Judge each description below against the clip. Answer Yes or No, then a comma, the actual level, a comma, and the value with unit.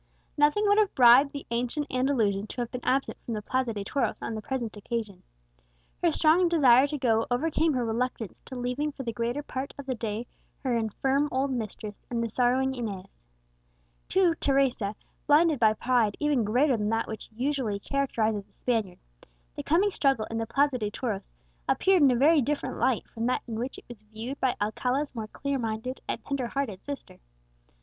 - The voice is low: No, very high, 250 Hz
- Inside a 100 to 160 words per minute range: No, average, 190 wpm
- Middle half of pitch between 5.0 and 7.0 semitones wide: No, average, 3.9 semitones